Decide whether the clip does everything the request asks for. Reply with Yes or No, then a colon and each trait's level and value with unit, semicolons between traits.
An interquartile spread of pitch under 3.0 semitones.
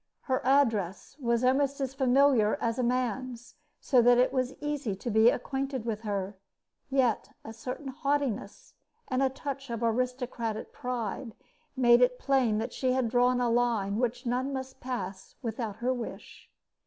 Yes: narrow, 2.4 semitones